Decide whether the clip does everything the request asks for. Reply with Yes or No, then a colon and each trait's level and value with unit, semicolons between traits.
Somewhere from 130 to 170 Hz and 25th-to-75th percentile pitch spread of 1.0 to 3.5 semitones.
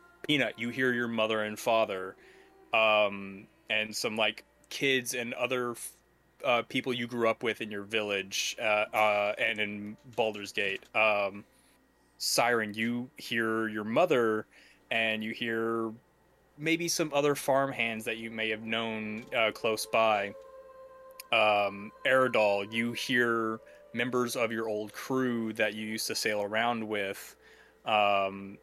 No: low, 115 Hz; narrow, 2.5 semitones